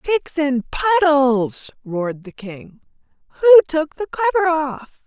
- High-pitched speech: Yes, very high, 295 Hz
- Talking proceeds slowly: Yes, slow, 130 wpm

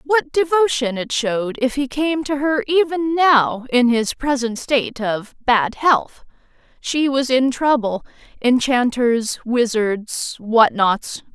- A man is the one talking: No, female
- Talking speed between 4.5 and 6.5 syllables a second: No, 3.6 syllables/s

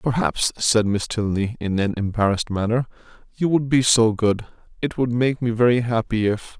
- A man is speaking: Yes, male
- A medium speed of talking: Yes, average, 175 wpm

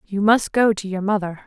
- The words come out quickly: Yes, fast, 245 wpm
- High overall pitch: Yes, high, 200 Hz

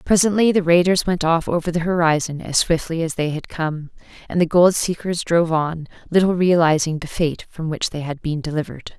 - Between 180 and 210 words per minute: Yes, average, 200 wpm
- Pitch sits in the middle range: Yes, medium, 165 Hz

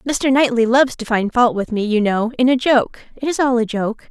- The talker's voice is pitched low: No, high, 240 Hz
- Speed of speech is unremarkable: No, fast, 235 wpm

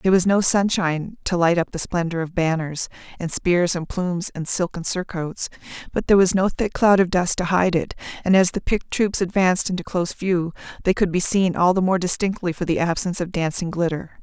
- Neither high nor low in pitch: Yes, medium, 180 Hz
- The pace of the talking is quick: Yes, fast, 220 wpm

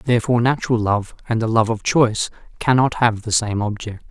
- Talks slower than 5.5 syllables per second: No, 5.8 syllables/s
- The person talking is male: Yes, male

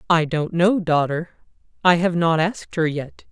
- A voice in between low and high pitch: Yes, medium, 165 Hz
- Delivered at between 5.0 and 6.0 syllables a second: No, 4.6 syllables/s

